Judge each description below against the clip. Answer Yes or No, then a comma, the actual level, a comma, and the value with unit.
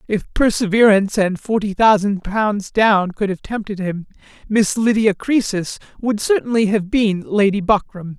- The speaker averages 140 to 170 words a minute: Yes, average, 145 wpm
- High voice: Yes, high, 205 Hz